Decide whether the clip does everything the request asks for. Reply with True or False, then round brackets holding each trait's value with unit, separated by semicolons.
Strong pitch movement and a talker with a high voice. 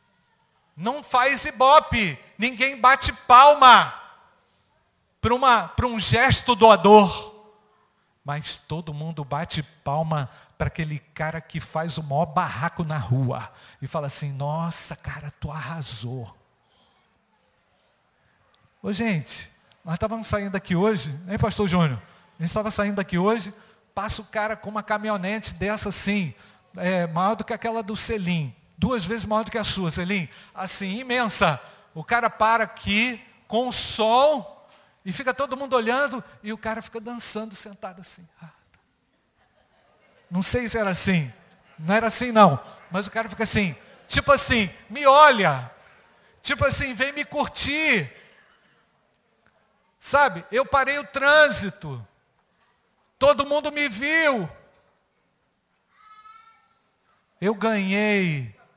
True (6.1 semitones; 205 Hz)